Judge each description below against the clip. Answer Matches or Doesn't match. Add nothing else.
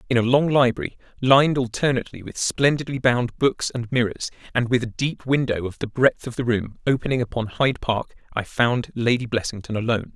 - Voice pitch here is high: Doesn't match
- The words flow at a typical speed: Matches